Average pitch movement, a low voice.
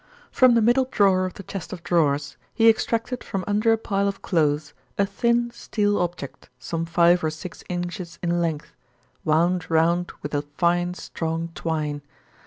No: average, 4.0 semitones; medium, 175 Hz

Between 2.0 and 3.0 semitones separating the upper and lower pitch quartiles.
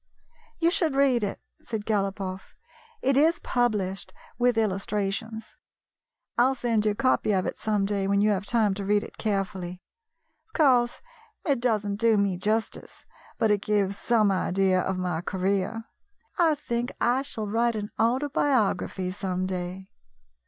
No: average, 3.7 semitones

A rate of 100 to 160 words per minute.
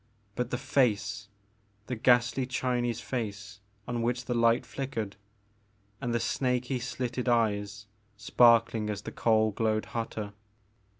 Yes: slow, 135 wpm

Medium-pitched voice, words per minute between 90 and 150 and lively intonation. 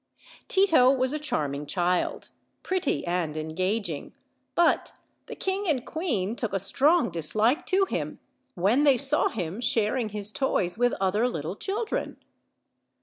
No: high, 225 Hz; average, 140 wpm; wide, 8.3 semitones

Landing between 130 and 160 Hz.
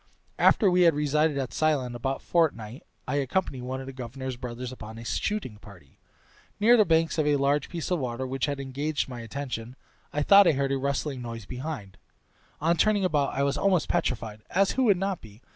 Yes: medium, 140 Hz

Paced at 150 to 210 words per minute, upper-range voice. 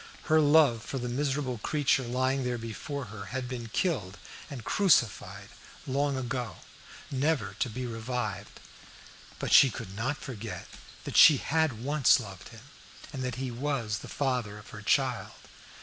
No: average, 155 wpm; low, 125 Hz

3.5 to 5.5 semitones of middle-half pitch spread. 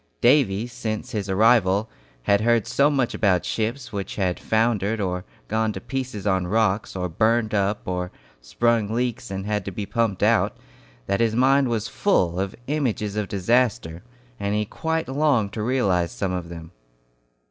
Yes: average, 3.8 semitones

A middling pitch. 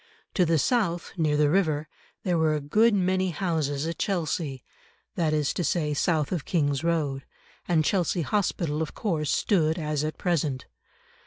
Yes: medium, 160 Hz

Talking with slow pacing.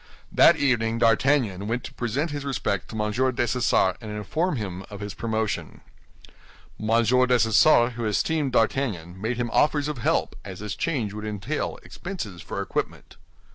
No: average, 155 wpm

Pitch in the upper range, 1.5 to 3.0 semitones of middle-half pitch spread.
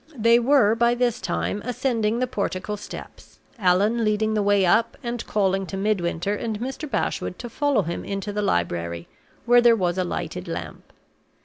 No: high, 210 Hz; average, 3.6 semitones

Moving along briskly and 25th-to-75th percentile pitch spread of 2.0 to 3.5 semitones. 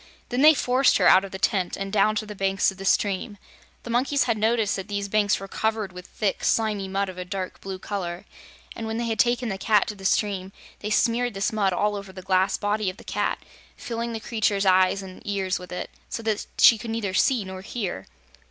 Yes: fast, 235 wpm; narrow, 2.6 semitones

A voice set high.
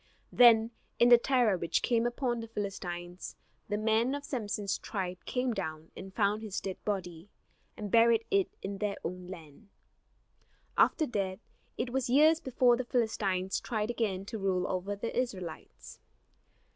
Yes: high, 210 Hz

